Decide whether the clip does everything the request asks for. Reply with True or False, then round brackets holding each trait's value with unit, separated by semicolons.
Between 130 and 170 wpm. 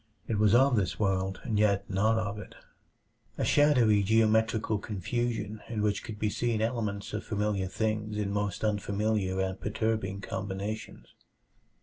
True (145 wpm)